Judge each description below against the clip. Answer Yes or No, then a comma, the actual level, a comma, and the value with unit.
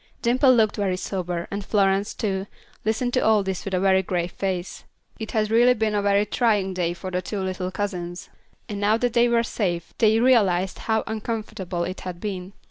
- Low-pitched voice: No, high, 200 Hz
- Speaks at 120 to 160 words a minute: No, average, 200 wpm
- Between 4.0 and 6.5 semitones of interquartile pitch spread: No, average, 3.0 semitones